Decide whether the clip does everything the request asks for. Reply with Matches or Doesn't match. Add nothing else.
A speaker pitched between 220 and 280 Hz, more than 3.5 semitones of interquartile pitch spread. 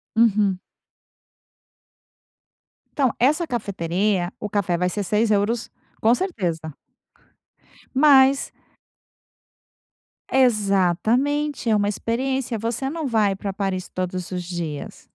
Doesn't match